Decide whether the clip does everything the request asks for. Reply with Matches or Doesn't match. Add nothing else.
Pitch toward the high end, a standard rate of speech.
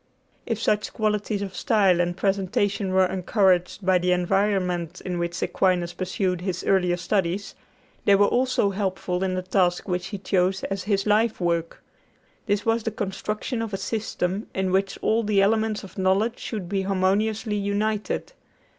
Matches